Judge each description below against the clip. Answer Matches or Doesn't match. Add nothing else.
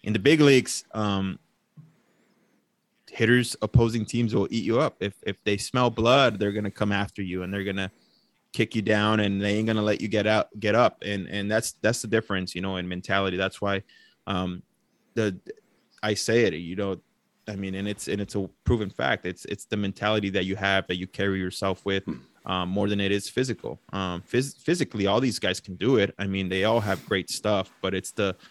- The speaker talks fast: Matches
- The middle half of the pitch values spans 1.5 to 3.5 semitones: Matches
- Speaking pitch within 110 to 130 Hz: Doesn't match